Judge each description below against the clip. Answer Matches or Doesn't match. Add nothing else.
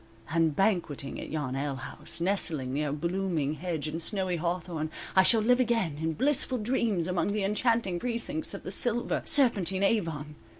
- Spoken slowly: Doesn't match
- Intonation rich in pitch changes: Matches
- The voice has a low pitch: Doesn't match